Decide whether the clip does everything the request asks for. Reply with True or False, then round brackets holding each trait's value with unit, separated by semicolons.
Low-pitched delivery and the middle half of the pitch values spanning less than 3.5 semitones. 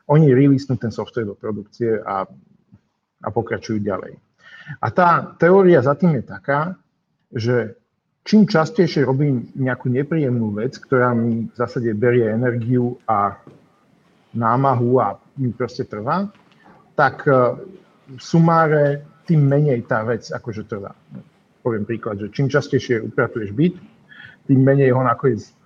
False (130 Hz; 4.8 semitones)